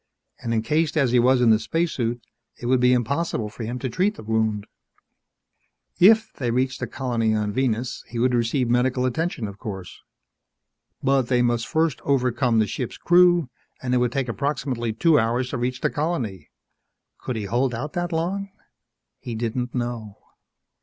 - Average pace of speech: Yes, average, 175 wpm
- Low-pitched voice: Yes, low, 125 Hz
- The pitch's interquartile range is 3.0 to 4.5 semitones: Yes, average, 3.3 semitones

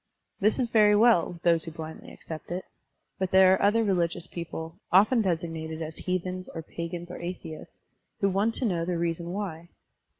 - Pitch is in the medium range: Yes, medium, 175 Hz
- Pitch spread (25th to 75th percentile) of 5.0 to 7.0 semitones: No, average, 2.9 semitones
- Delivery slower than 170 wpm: No, average, 180 wpm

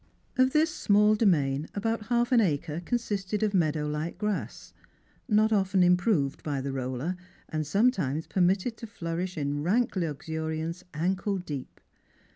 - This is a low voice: No, medium, 180 Hz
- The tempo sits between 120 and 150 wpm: Yes, average, 140 wpm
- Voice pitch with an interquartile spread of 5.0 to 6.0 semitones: Yes, wide, 5.6 semitones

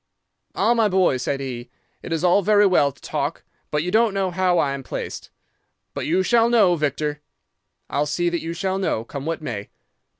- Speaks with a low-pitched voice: No, medium, 175 Hz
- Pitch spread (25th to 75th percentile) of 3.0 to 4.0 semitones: No, average, 4.9 semitones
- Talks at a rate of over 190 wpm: Yes, average, 200 wpm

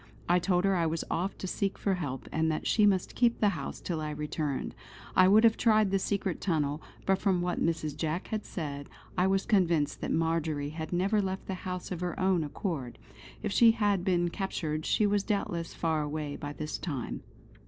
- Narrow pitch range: No, average, 3.9 semitones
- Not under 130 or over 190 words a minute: No, fast, 205 wpm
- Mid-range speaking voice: Yes, medium, 175 Hz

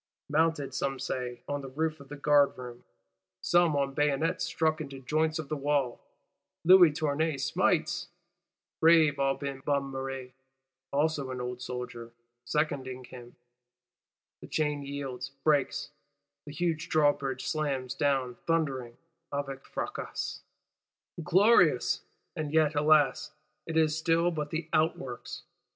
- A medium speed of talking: No, slow, 125 wpm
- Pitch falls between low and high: Yes, medium, 145 Hz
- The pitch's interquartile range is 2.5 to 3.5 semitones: Yes, average, 2.8 semitones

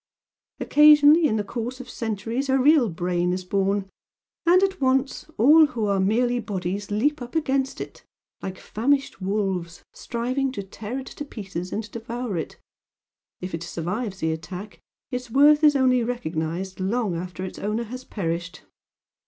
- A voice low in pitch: No, high, 220 Hz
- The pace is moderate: Yes, average, 160 wpm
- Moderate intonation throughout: No, wide, 5.7 semitones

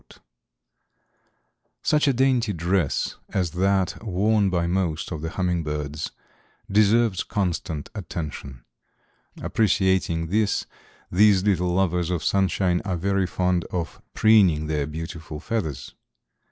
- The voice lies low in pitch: Yes, very low, 90 Hz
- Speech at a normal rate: No, slow, 115 wpm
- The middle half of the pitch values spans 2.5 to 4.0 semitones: Yes, average, 3.5 semitones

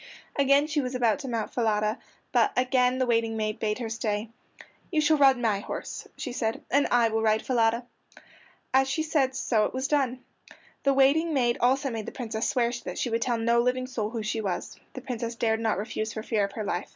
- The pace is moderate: No, fast, 220 wpm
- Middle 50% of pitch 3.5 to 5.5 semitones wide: No, average, 3.0 semitones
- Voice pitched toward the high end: Yes, high, 240 Hz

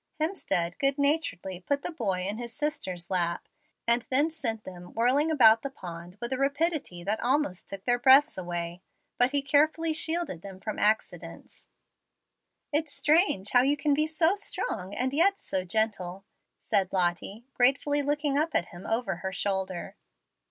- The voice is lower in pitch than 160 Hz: No, high, 240 Hz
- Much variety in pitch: Yes, wide, 7.7 semitones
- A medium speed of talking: Yes, average, 165 wpm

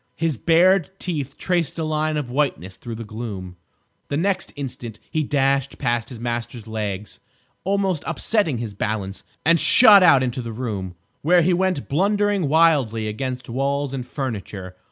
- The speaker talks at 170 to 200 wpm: No, average, 155 wpm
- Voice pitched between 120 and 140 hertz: Yes, low, 135 Hz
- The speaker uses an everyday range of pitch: No, wide, 6.4 semitones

